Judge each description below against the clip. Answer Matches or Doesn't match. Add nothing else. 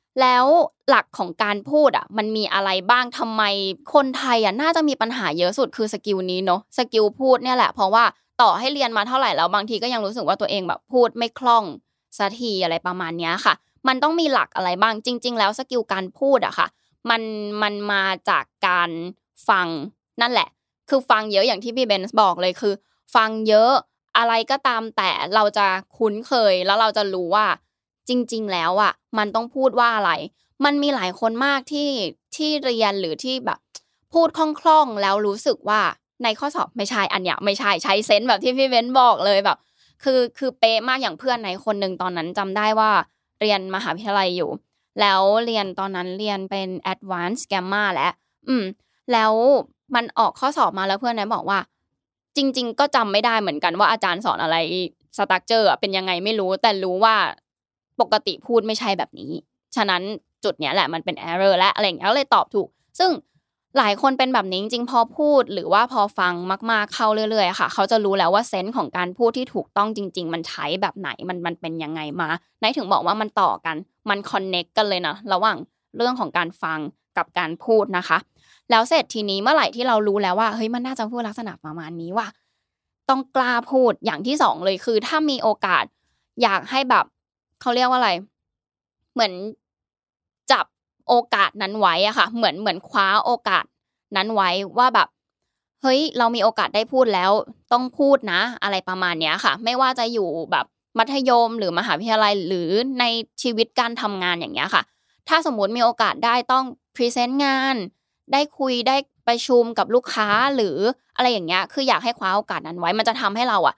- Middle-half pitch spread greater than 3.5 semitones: Matches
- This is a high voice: Matches